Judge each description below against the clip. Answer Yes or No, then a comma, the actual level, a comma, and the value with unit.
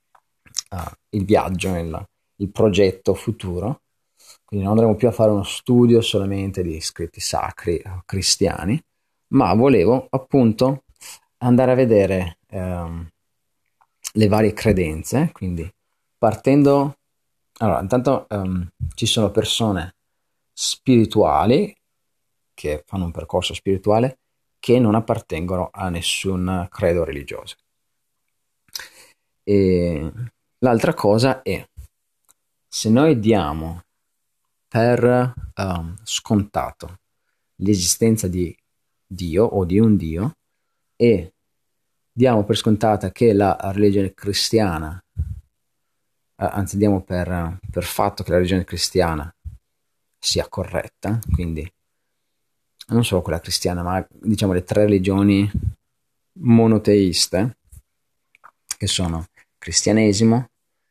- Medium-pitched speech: No, low, 100 Hz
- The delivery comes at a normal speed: No, slow, 100 wpm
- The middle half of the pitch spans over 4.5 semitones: No, average, 3.9 semitones